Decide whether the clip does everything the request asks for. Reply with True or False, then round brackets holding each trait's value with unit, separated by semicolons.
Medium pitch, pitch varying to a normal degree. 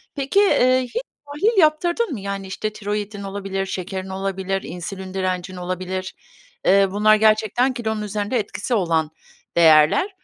False (200 Hz; 4.1 semitones)